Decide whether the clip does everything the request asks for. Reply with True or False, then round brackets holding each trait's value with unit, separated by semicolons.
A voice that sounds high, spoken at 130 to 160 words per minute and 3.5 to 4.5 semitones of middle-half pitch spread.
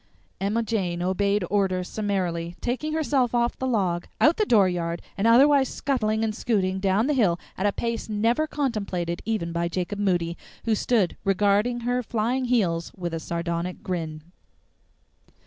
False (205 Hz; 155 wpm; 5.0 semitones)